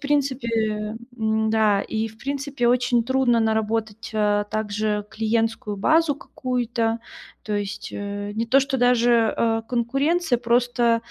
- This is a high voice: Yes, high, 230 Hz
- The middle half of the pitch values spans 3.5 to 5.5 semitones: No, narrow, 2.4 semitones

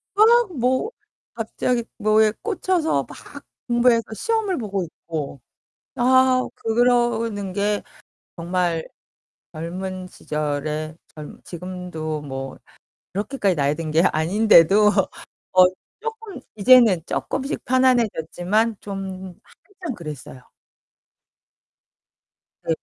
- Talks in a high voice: Yes, high, 205 Hz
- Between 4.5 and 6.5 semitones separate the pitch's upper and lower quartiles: No, wide, 7.1 semitones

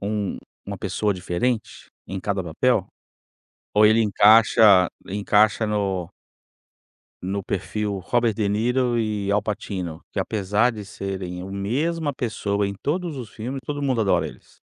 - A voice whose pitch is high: No, low, 105 Hz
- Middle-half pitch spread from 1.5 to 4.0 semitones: Yes, average, 2.9 semitones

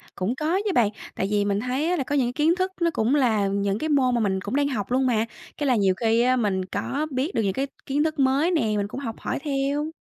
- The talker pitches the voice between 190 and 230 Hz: No, very high, 255 Hz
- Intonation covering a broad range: Yes, wide, 5.7 semitones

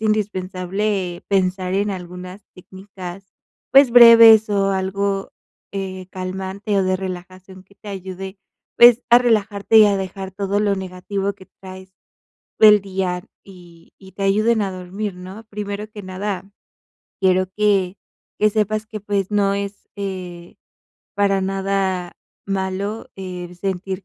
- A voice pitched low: No, high, 195 Hz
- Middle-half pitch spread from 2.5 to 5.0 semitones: No, narrow, 1.7 semitones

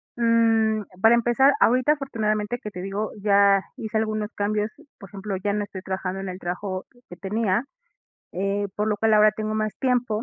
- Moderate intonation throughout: No, narrow, 2.1 semitones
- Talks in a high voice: Yes, high, 210 Hz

